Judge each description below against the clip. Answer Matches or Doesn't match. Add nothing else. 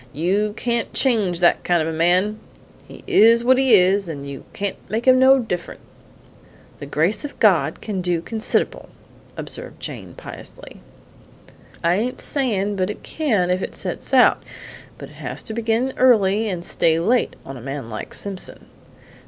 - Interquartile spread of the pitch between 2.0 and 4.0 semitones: Doesn't match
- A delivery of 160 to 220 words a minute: Matches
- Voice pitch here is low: Doesn't match